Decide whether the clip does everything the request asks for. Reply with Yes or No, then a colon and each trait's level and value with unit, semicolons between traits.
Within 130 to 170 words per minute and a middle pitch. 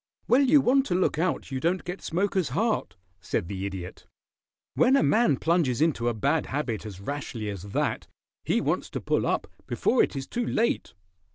No: average, 190 wpm; medium, 155 Hz